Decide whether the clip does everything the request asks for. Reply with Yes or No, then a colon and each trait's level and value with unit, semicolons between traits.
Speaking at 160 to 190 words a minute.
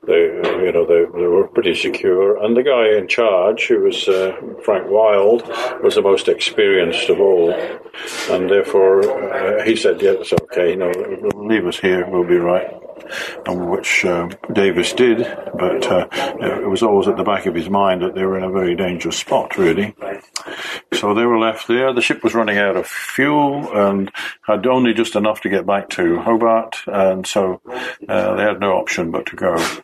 No: average, 200 wpm